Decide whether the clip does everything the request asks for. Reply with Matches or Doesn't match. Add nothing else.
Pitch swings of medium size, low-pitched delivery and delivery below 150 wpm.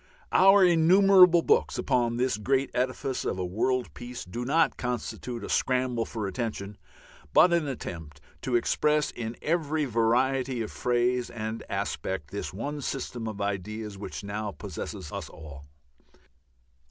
Matches